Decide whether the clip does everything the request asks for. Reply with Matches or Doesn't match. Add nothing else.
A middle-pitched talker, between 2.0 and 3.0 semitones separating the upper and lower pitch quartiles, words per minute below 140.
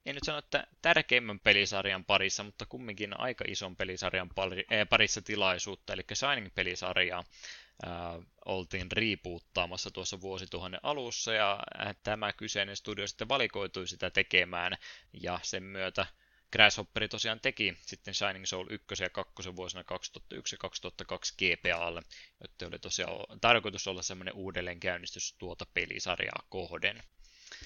Doesn't match